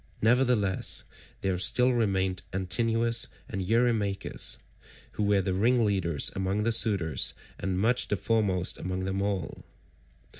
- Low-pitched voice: Yes, low, 100 Hz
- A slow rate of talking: Yes, slow, 120 wpm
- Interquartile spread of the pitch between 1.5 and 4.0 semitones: Yes, average, 3.4 semitones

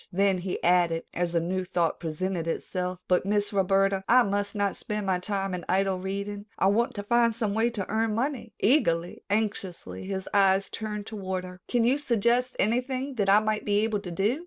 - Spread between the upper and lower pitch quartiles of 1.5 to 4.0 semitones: Yes, average, 2.9 semitones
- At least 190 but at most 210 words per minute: Yes, average, 200 wpm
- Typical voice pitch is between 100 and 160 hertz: No, high, 200 Hz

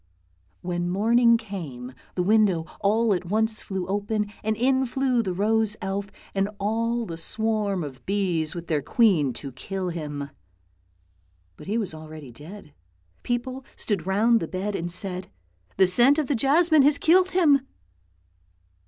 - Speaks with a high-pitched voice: Yes, high, 200 Hz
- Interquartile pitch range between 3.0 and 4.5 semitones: No, average, 5.0 semitones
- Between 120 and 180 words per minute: Yes, average, 155 wpm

